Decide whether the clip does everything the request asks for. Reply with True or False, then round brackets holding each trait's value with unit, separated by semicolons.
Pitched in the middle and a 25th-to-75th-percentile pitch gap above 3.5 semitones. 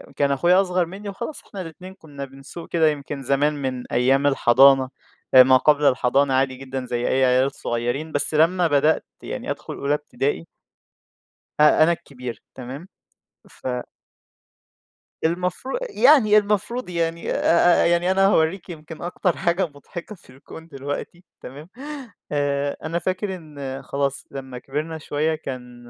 True (150 Hz; 4.2 semitones)